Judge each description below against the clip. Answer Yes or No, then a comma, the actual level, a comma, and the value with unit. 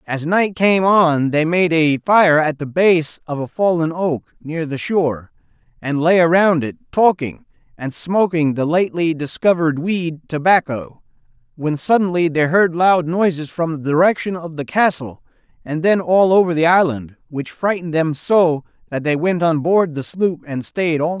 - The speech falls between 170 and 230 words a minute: Yes, average, 180 wpm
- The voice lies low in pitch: No, medium, 165 Hz